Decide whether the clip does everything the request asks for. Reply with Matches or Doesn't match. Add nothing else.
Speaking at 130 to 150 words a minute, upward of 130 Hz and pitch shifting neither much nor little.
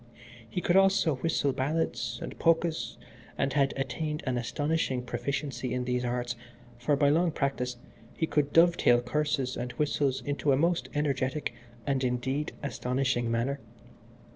Matches